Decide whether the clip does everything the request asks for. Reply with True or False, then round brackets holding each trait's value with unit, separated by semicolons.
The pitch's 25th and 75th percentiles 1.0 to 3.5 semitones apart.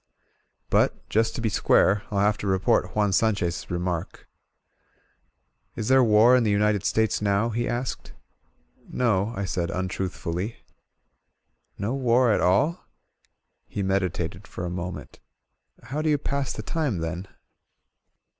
False (4.0 semitones)